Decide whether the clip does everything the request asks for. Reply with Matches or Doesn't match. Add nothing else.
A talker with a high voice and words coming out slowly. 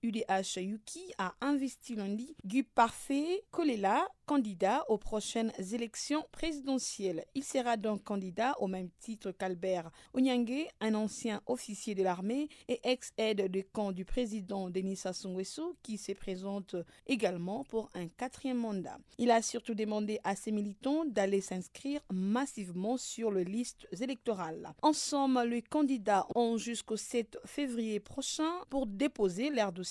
Matches